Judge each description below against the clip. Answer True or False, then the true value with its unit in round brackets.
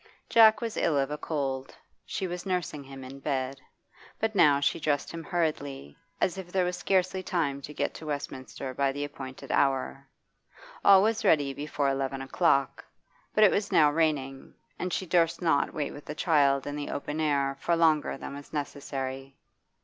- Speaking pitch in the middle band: True (145 Hz)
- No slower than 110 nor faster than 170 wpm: False (180 wpm)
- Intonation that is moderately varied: True (3.8 semitones)